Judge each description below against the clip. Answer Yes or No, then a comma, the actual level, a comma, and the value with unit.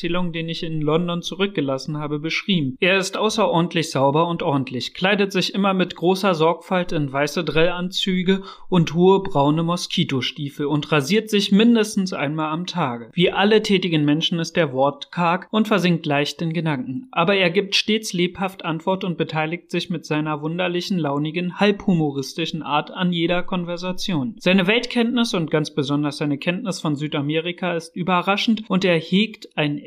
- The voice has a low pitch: No, medium, 175 Hz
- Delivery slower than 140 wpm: No, average, 160 wpm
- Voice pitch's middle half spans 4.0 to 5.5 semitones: No, average, 3.5 semitones